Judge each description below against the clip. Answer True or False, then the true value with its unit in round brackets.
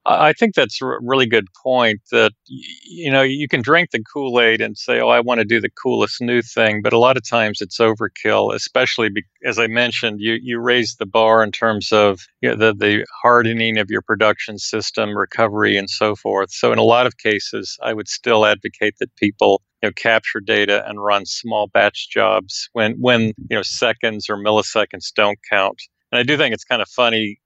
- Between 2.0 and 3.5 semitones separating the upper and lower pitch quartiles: True (2.5 semitones)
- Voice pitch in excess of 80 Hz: True (115 Hz)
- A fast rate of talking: True (210 wpm)